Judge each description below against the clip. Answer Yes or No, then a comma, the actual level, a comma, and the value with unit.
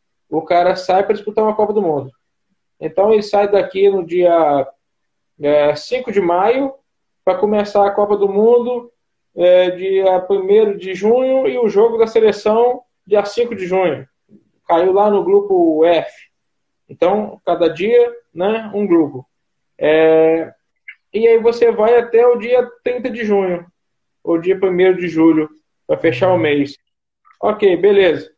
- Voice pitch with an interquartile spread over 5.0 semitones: Yes, wide, 5.5 semitones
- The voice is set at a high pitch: Yes, high, 200 Hz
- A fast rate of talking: No, average, 145 wpm